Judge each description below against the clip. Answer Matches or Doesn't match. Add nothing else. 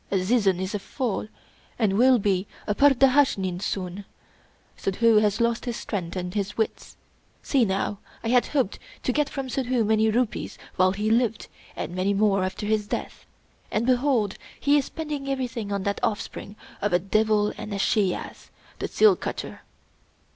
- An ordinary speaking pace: Matches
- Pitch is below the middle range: Doesn't match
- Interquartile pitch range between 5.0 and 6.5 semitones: Doesn't match